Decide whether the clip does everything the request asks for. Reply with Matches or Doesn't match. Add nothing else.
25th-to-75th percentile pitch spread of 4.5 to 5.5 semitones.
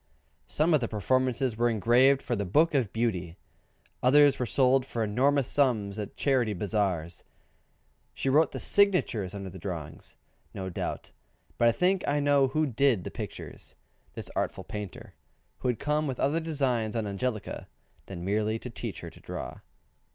Matches